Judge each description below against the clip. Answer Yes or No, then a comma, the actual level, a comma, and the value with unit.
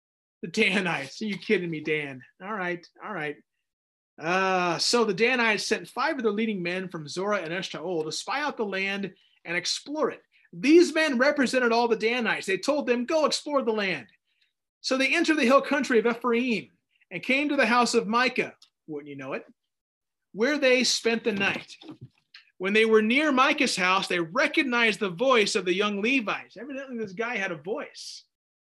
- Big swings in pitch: Yes, wide, 5.8 semitones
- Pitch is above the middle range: Yes, high, 220 Hz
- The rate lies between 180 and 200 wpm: Yes, average, 190 wpm